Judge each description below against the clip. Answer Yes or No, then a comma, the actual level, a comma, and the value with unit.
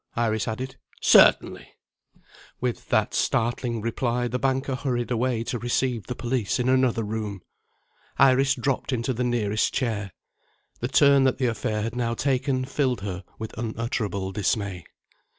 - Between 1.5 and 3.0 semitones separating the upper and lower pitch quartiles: Yes, average, 2.7 semitones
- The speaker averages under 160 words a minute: Yes, average, 145 wpm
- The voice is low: Yes, low, 120 Hz